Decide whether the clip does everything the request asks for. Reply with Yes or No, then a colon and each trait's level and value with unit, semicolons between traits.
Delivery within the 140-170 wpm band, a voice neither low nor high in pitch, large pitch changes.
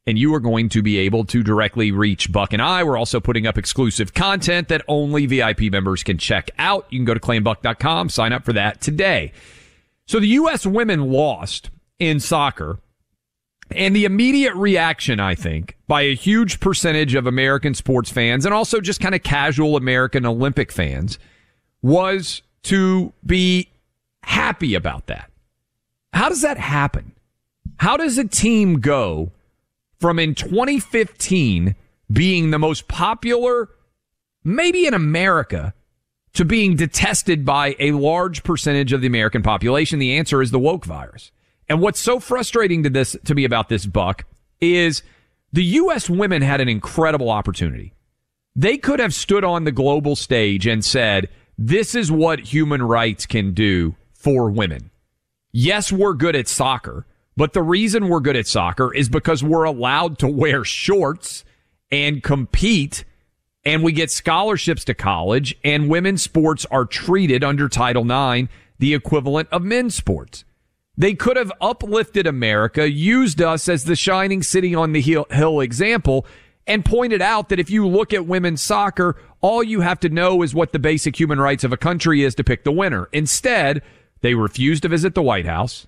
Yes: average, 165 wpm; medium, 145 Hz; wide, 7.6 semitones